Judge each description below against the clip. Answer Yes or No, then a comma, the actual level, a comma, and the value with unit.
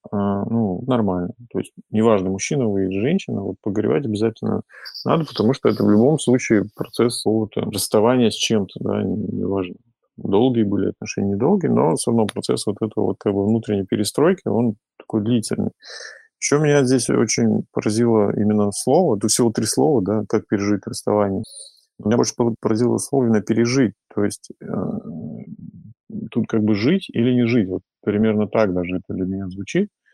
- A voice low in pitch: Yes, low, 110 Hz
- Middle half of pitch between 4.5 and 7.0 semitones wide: No, narrow, 2.6 semitones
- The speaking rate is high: Yes, fast, 165 wpm